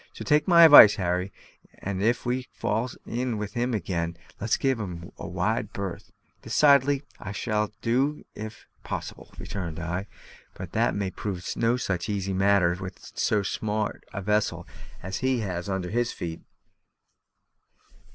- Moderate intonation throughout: Yes, average, 4.4 semitones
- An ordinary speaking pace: Yes, average, 155 wpm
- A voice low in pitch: Yes, low, 105 Hz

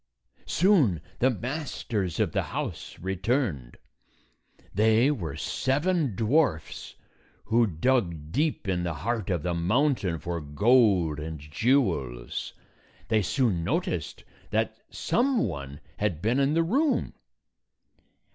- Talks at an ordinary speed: No, slow, 115 wpm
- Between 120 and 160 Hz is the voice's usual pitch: No, low, 105 Hz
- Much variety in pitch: Yes, wide, 8.4 semitones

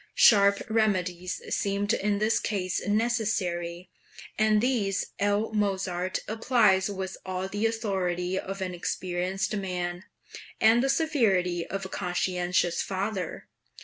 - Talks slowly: Yes, slow, 115 wpm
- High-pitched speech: Yes, high, 195 Hz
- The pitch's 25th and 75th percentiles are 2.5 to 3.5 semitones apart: Yes, average, 2.8 semitones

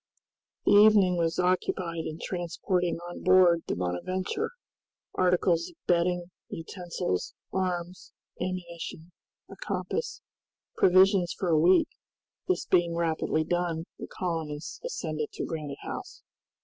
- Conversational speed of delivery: No, slow, 115 wpm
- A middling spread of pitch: No, narrow, 2.0 semitones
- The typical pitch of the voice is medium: Yes, medium, 175 Hz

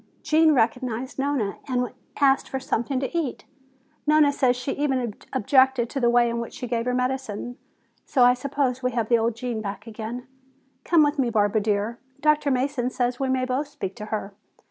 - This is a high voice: Yes, very high, 250 Hz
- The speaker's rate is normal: Yes, average, 190 wpm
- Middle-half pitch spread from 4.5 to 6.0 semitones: No, average, 2.7 semitones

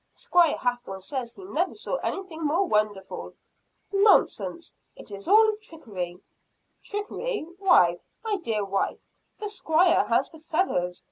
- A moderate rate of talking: No, slow, 130 wpm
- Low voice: No, very high, 320 Hz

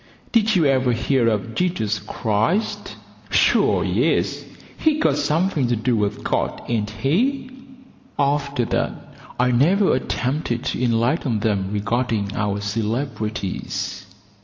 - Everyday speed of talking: No, slow, 120 wpm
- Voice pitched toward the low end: Yes, low, 120 Hz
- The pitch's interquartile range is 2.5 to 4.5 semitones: No, average, 5.3 semitones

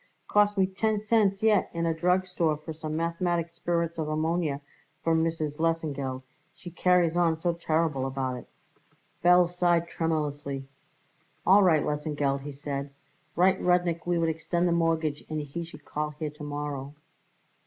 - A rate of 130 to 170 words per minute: Yes, average, 160 wpm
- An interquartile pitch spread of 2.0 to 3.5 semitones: Yes, average, 2.8 semitones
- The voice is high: No, medium, 165 Hz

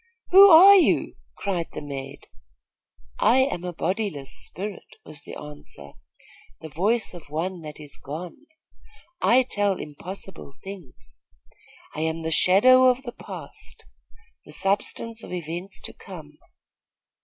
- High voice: No, medium, 180 Hz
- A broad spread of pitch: Yes, wide, 6.5 semitones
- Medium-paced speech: No, slow, 130 wpm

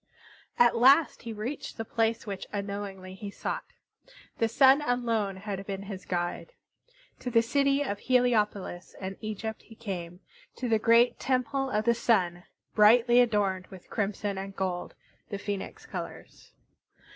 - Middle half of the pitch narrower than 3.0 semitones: No, average, 3.6 semitones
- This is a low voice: No, high, 215 Hz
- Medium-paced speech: Yes, average, 145 wpm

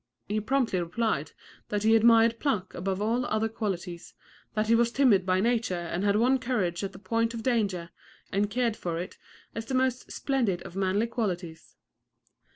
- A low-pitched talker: No, high, 215 Hz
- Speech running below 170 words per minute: No, average, 175 wpm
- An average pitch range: Yes, average, 3.8 semitones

